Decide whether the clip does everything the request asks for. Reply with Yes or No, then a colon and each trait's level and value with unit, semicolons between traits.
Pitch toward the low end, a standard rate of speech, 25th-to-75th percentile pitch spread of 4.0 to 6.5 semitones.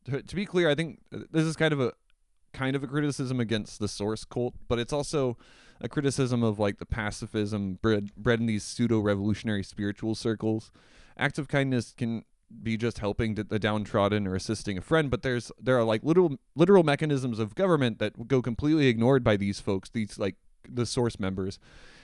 Yes: low, 115 Hz; average, 190 wpm; average, 4.4 semitones